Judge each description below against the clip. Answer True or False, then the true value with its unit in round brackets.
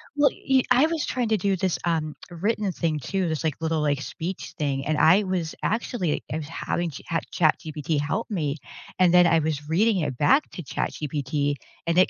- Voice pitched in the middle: True (165 Hz)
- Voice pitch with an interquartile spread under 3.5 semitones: False (4.3 semitones)